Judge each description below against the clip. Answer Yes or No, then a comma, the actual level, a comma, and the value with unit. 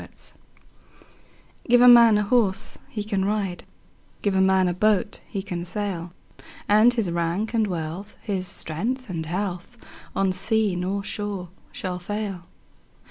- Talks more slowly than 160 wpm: Yes, average, 145 wpm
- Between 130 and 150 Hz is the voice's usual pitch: No, high, 195 Hz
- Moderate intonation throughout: Yes, average, 3.0 semitones